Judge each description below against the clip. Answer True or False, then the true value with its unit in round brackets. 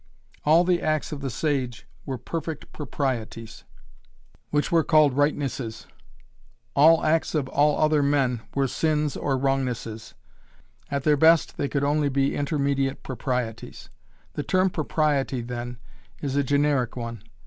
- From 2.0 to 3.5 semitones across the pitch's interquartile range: True (2.9 semitones)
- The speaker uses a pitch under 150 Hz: True (140 Hz)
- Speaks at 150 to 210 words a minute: False (135 wpm)